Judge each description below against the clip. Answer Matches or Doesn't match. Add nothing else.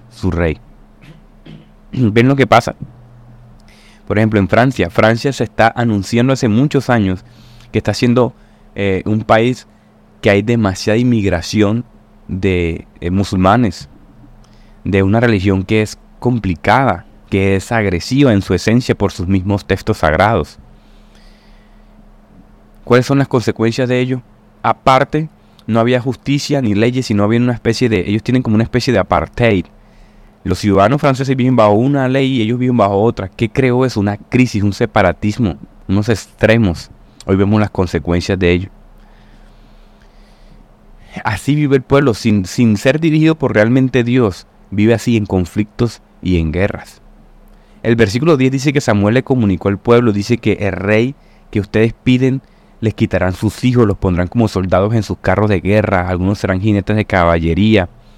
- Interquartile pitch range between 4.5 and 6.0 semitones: Doesn't match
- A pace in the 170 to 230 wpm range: Doesn't match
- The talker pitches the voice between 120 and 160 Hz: Doesn't match